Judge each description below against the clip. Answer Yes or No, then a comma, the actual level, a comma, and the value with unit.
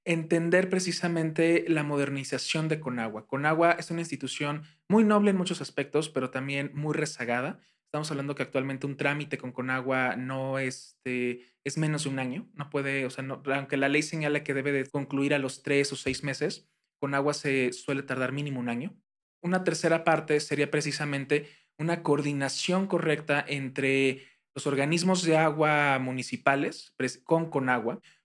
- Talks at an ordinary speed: Yes, average, 165 wpm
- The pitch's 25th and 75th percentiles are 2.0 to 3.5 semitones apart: Yes, average, 2.8 semitones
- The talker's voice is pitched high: No, medium, 145 Hz